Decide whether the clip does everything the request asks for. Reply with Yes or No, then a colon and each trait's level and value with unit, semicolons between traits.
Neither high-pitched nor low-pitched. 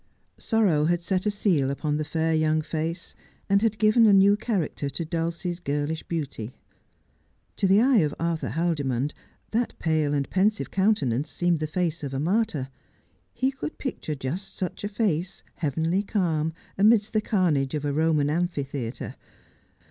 Yes: medium, 165 Hz